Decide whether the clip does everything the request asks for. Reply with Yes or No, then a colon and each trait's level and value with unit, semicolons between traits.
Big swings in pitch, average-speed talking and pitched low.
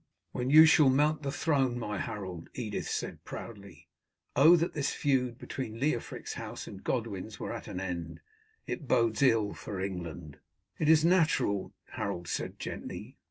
Yes: wide, 7.1 semitones; average, 160 wpm; low, 120 Hz